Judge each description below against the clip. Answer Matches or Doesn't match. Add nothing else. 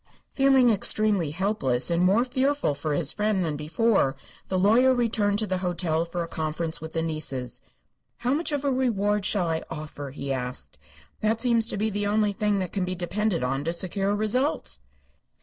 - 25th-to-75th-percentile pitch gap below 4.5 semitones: Doesn't match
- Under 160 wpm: Doesn't match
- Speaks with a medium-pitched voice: Doesn't match